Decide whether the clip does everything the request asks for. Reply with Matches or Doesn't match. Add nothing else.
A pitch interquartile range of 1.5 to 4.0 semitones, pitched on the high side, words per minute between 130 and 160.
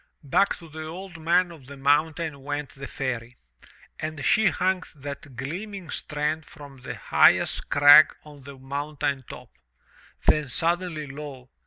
Doesn't match